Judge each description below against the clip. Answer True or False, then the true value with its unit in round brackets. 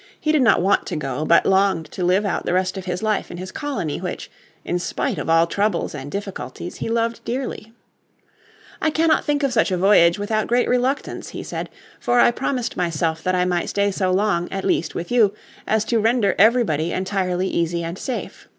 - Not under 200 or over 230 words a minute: True (205 wpm)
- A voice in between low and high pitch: False (195 Hz)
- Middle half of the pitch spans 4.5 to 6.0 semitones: True (4.8 semitones)